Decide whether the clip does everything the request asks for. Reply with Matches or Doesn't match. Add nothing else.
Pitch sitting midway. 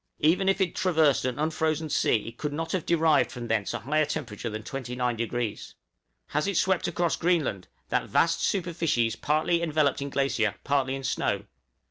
Matches